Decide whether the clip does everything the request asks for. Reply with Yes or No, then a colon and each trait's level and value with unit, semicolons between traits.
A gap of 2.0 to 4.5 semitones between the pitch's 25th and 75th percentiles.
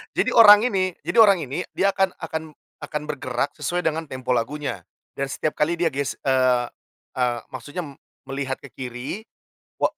No: average, 4.9 semitones